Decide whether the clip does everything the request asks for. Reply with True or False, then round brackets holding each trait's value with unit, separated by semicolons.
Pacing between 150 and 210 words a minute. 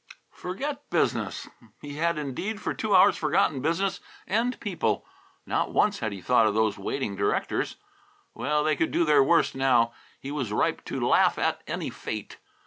True (170 wpm)